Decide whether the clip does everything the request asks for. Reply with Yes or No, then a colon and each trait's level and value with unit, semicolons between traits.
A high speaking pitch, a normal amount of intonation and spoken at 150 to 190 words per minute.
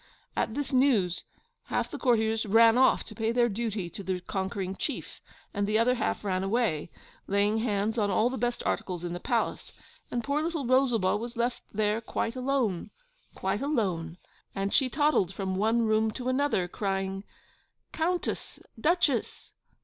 Yes: high, 220 Hz; average, 4.3 semitones; average, 165 wpm